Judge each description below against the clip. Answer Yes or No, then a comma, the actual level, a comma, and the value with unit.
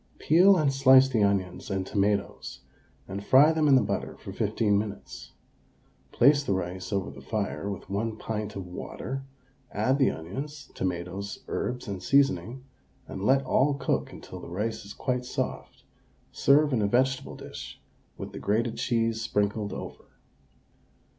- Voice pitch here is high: No, low, 110 Hz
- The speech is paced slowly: No, average, 155 wpm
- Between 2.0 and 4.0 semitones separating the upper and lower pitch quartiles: No, average, 5.0 semitones